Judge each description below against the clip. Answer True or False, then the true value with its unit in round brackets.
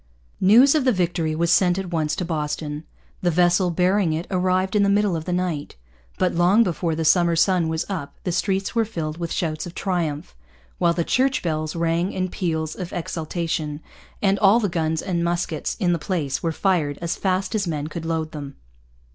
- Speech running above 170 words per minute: True (200 wpm)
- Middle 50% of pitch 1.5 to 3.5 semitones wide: True (2.8 semitones)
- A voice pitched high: False (175 Hz)